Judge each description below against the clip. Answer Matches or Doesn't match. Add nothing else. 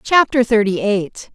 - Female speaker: Matches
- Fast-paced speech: Doesn't match